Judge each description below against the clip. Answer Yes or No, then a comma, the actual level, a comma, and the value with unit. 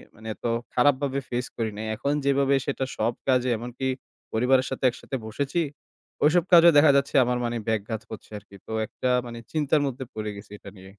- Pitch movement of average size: Yes, average, 3.8 semitones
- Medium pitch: No, low, 125 Hz